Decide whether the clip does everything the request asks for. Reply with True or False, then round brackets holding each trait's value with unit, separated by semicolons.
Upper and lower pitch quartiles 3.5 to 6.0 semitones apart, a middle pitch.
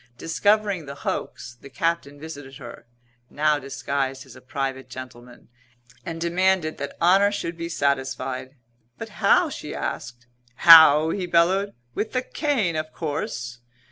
True (4.5 semitones; 150 Hz)